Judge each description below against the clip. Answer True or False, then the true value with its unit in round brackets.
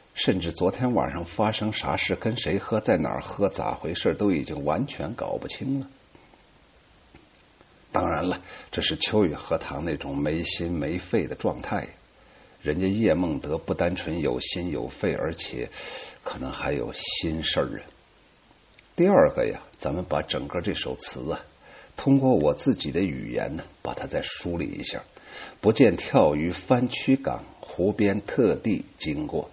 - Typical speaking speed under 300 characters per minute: True (225 characters per minute)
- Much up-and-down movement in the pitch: True (7.3 semitones)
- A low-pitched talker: True (95 Hz)